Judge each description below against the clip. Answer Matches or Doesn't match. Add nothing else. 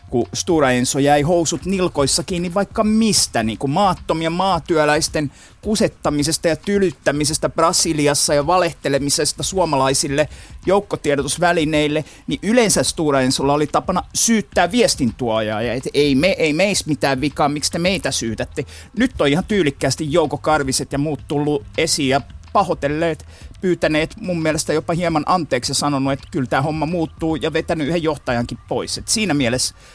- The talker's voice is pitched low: Doesn't match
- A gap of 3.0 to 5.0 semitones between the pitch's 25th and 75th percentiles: Matches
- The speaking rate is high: Doesn't match